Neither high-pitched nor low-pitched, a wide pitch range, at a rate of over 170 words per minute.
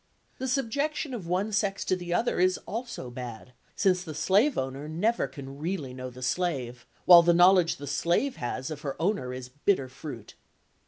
Yes: medium, 170 Hz; wide, 6.9 semitones; average, 180 wpm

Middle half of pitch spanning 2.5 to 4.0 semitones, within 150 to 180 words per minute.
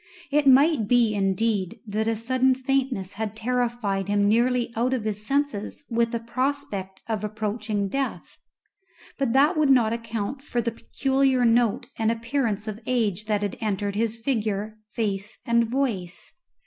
Yes: average, 3.4 semitones; average, 155 wpm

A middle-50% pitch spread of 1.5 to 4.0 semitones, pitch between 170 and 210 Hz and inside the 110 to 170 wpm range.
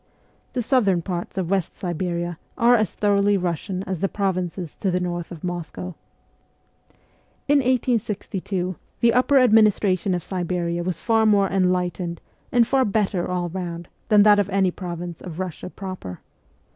Yes: average, 2.9 semitones; medium, 185 Hz; average, 150 wpm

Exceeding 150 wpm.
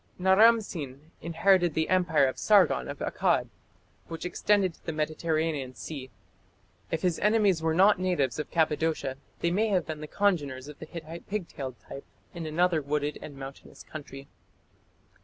Yes: average, 160 wpm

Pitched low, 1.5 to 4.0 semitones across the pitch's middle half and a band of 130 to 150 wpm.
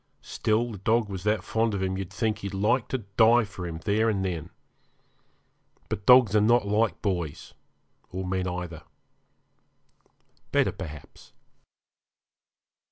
Yes: low, 100 Hz; average, 3.1 semitones; average, 140 wpm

